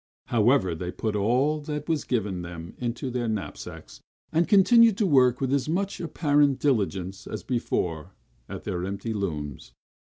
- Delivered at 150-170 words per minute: Yes, average, 155 wpm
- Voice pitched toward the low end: Yes, low, 120 Hz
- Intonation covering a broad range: Yes, wide, 7.5 semitones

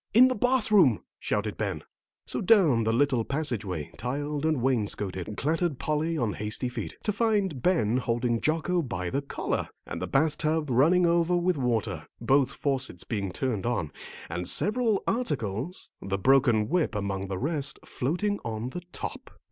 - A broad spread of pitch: Yes, wide, 7.4 semitones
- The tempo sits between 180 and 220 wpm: No, average, 165 wpm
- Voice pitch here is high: No, low, 135 Hz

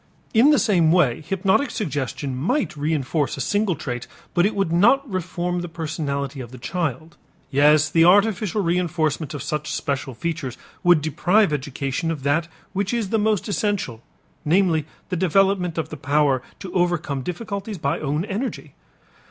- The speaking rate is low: No, average, 155 wpm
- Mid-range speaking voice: Yes, medium, 165 Hz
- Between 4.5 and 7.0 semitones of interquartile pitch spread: Yes, average, 5.1 semitones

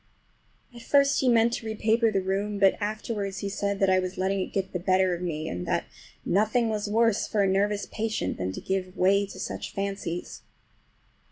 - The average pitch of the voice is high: Yes, high, 200 Hz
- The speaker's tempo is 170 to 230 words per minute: Yes, average, 200 wpm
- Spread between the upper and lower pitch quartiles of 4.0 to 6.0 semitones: No, narrow, 2.5 semitones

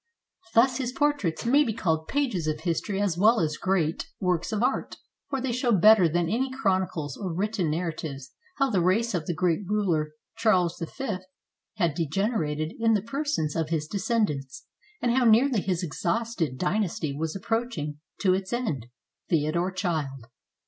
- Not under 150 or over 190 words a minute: Yes, average, 170 wpm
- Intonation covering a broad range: Yes, wide, 6.1 semitones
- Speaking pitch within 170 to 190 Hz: Yes, medium, 185 Hz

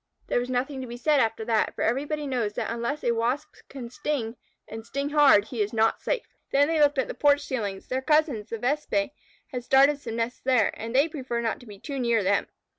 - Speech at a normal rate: No, fast, 230 wpm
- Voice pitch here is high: Yes, very high, 255 Hz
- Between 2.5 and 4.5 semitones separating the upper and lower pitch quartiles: Yes, average, 4.0 semitones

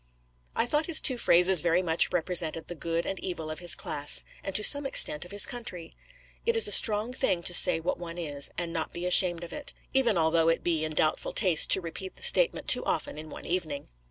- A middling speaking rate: No, fast, 230 wpm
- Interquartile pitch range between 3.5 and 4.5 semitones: Yes, average, 3.8 semitones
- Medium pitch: Yes, medium, 175 Hz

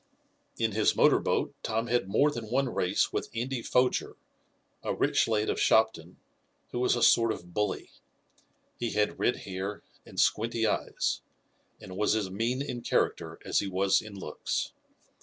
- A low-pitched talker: Yes, low, 110 Hz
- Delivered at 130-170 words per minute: Yes, average, 165 wpm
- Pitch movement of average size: Yes, average, 3.2 semitones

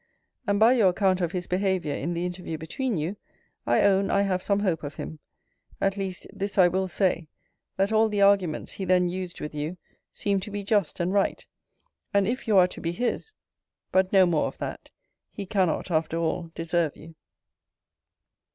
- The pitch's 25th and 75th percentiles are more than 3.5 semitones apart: No, average, 2.7 semitones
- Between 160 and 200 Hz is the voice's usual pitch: Yes, medium, 185 Hz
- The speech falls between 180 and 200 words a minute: Yes, average, 190 wpm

